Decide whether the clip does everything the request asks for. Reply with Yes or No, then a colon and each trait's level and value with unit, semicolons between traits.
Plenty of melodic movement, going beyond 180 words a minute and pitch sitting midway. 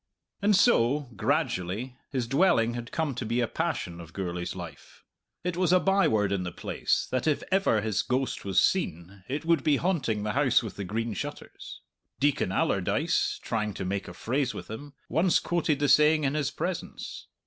No: wide, 7.0 semitones; average, 190 wpm; low, 125 Hz